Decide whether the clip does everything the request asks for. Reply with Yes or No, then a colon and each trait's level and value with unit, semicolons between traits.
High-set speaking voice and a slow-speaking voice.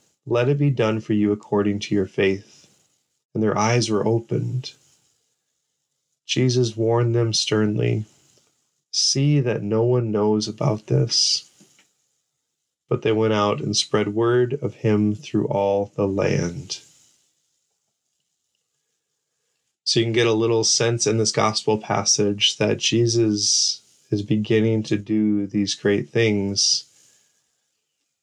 No: low, 110 Hz; slow, 125 wpm